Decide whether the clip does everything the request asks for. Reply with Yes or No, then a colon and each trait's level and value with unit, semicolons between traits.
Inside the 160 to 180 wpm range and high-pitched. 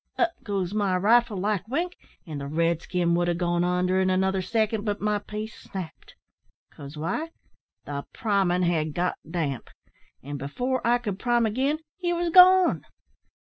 Yes: average, 165 wpm; high, 195 Hz